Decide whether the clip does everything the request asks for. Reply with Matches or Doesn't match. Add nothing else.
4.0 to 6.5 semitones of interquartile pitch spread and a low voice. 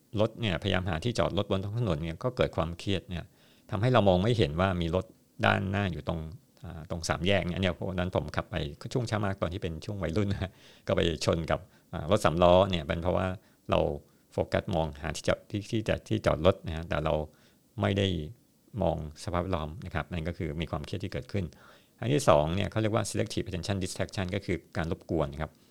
Doesn't match